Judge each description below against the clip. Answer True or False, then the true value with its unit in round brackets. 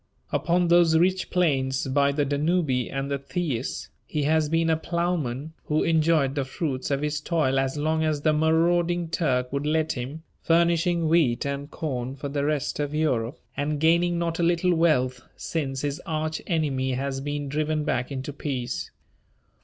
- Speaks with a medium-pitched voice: True (150 Hz)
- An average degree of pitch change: True (3.2 semitones)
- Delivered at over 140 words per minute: True (170 wpm)